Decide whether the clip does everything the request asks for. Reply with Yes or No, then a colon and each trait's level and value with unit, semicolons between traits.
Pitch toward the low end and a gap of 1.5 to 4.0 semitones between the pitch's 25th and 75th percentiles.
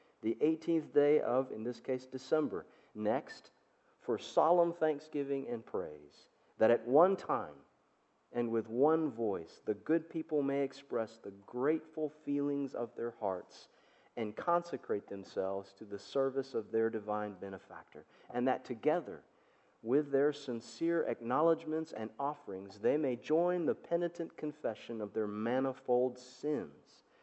No: low, 130 Hz; average, 5.3 semitones